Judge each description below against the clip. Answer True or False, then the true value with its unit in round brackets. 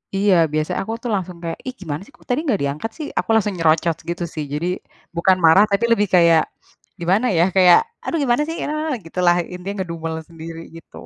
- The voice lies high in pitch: False (180 Hz)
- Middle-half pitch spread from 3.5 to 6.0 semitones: True (4.1 semitones)